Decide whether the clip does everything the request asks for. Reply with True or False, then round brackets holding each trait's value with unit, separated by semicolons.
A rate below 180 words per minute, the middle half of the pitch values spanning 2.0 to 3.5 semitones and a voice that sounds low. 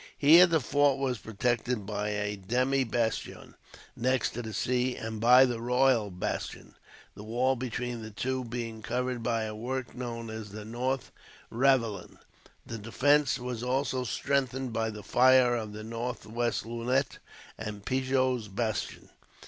True (150 wpm; 2.7 semitones; 120 Hz)